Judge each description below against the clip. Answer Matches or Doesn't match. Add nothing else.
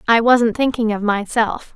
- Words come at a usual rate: Matches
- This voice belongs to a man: Doesn't match